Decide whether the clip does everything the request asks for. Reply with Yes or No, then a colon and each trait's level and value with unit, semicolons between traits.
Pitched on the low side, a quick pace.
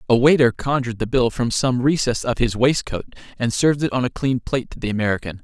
Yes: low, 125 Hz; fast, 230 wpm